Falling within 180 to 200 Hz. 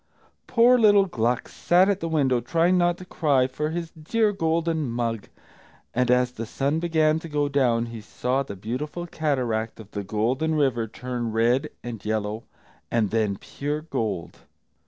No: low, 135 Hz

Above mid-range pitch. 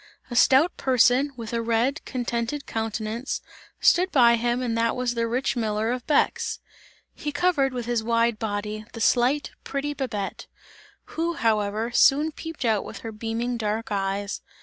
Yes: high, 235 Hz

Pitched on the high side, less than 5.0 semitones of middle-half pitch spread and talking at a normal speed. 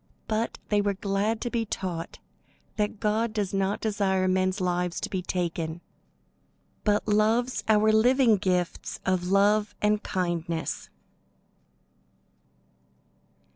No: high, 200 Hz; average, 2.7 semitones; slow, 115 wpm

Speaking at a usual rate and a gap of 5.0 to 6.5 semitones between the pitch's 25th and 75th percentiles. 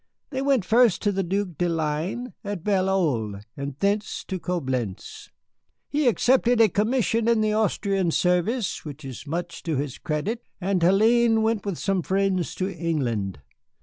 Yes: average, 160 wpm; wide, 5.4 semitones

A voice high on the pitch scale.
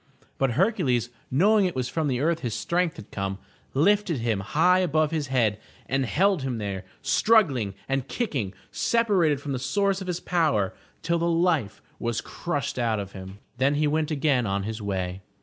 No: medium, 140 Hz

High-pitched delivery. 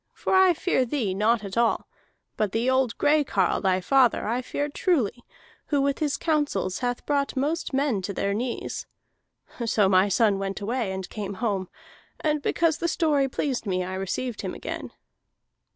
Yes: high, 240 Hz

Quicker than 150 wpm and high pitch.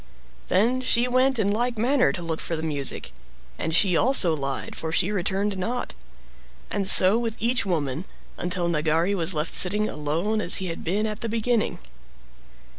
Yes: average, 175 wpm; high, 195 Hz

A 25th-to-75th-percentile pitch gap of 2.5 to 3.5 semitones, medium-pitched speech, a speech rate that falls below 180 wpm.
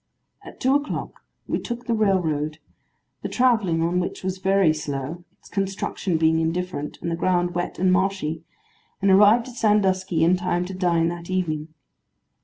Yes: average, 2.9 semitones; medium, 180 Hz; average, 165 wpm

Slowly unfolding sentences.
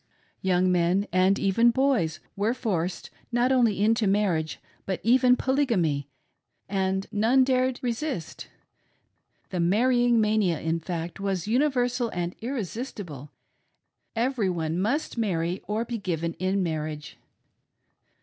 Yes: slow, 120 wpm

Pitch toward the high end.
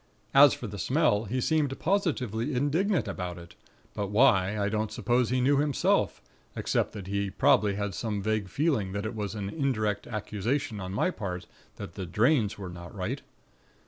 No: low, 110 Hz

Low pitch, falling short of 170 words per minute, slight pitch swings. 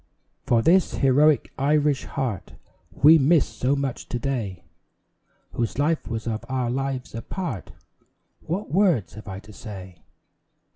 No: low, 130 Hz; average, 140 wpm; average, 4.9 semitones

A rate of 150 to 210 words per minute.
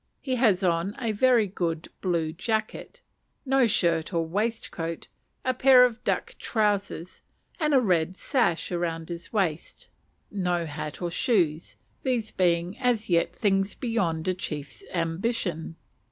No: average, 140 wpm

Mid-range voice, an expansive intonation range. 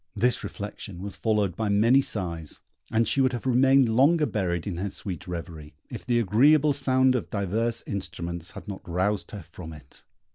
No: low, 105 Hz; wide, 5.9 semitones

